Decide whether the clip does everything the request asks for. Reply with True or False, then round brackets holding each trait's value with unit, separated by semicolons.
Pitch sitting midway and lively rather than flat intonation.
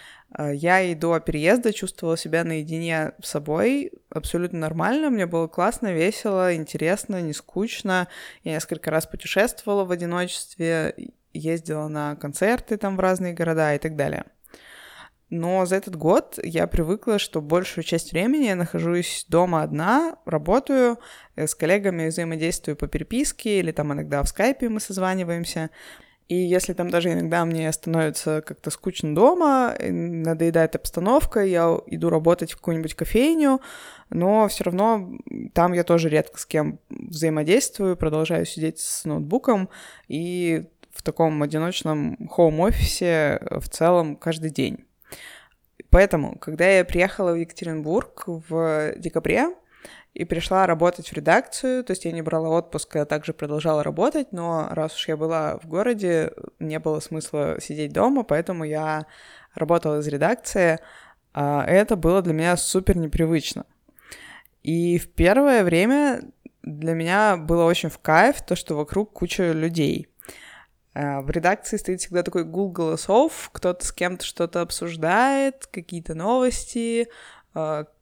False (170 Hz; 3.4 semitones)